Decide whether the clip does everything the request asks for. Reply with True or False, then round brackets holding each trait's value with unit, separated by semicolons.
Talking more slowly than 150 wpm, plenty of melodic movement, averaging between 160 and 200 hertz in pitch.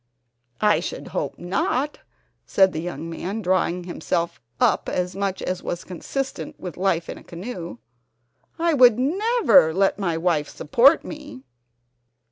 True (140 wpm; 6.3 semitones; 190 Hz)